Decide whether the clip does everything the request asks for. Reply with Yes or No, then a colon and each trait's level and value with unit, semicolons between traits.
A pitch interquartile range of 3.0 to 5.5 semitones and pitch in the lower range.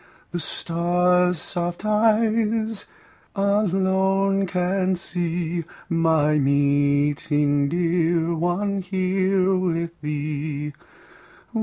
No: average, 3.3 semitones; medium, 175 Hz